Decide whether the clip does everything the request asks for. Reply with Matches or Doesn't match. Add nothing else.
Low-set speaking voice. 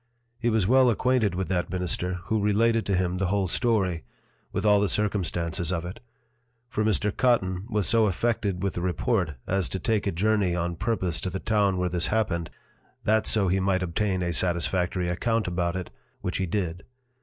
Matches